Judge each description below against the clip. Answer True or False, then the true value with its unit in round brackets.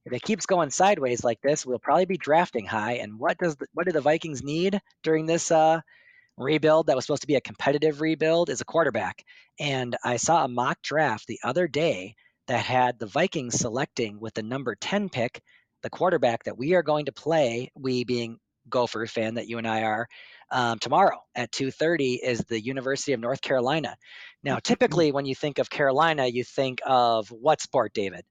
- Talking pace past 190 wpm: True (205 wpm)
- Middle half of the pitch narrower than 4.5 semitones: False (5.0 semitones)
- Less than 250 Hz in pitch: True (140 Hz)